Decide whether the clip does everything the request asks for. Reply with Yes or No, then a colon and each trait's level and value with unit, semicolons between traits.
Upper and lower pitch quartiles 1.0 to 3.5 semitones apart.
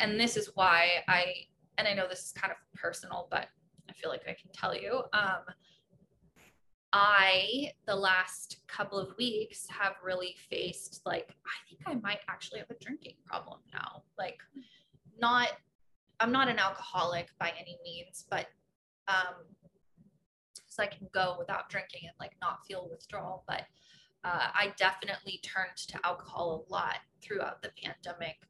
Yes: narrow, 2.5 semitones